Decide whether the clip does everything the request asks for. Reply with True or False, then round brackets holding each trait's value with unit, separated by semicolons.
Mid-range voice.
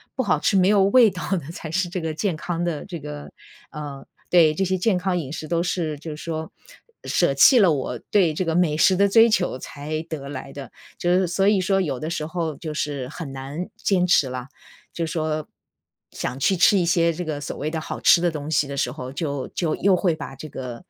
True (160 Hz)